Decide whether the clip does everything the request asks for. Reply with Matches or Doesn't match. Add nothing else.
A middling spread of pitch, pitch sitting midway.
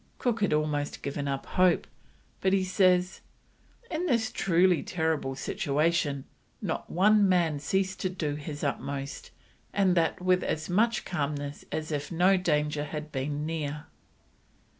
Matches